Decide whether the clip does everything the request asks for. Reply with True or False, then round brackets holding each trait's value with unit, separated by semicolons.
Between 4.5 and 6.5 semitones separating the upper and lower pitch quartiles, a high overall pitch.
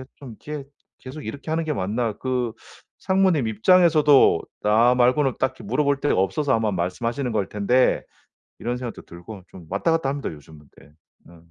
False (5.5 semitones; 125 Hz)